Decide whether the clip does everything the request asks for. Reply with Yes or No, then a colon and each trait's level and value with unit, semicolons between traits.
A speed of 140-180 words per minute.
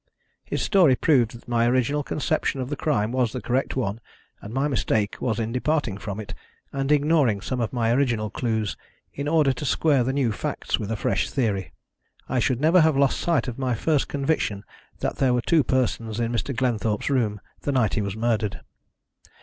No: average, 200 wpm